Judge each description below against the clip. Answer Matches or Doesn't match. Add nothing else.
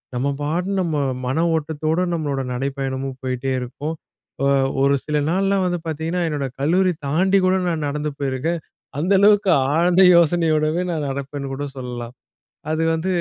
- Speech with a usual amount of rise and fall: Matches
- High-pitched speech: Doesn't match